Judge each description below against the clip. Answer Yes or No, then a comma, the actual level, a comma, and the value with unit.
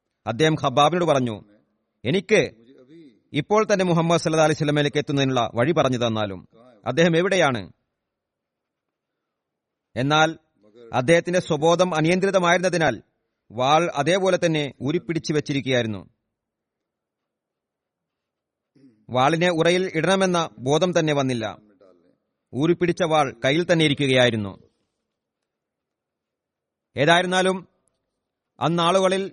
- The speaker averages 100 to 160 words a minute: No, average, 80 wpm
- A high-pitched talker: No, medium, 155 Hz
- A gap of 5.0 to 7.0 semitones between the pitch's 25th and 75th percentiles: Yes, wide, 5.5 semitones